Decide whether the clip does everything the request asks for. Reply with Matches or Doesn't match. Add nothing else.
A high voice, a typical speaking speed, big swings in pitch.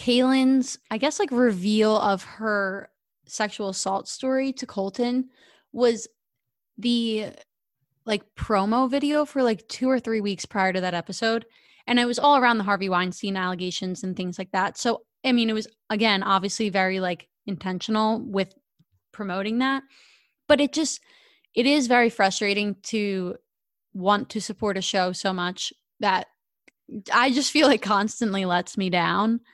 Doesn't match